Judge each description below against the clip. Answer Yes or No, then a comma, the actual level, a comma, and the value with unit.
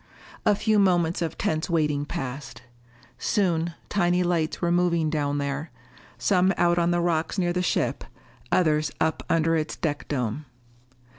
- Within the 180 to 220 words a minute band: No, average, 150 wpm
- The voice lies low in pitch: No, medium, 165 Hz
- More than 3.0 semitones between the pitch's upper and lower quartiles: No, narrow, 2.6 semitones